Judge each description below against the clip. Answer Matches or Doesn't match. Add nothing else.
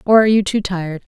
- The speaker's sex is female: Matches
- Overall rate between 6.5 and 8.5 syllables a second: Matches